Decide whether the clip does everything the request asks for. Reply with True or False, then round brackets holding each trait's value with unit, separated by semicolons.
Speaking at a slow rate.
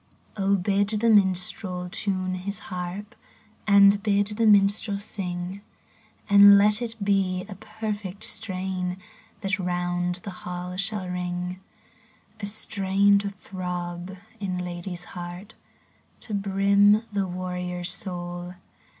True (115 wpm)